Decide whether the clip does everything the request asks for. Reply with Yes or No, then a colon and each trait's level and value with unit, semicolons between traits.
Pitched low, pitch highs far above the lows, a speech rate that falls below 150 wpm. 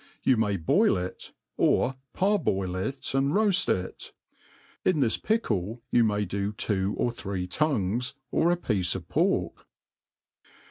Yes: low, 110 Hz; wide, 6.4 semitones; average, 140 wpm